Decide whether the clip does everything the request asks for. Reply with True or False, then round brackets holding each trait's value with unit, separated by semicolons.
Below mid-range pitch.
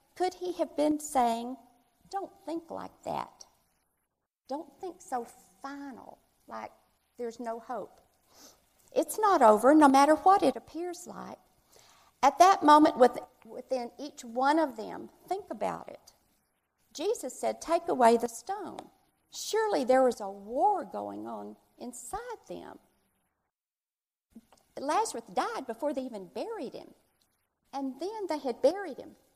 False (280 Hz)